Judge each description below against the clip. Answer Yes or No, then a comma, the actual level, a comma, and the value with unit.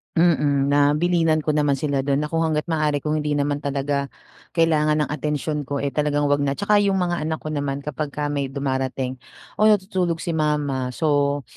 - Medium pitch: Yes, medium, 150 Hz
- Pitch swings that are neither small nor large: No, narrow, 1.9 semitones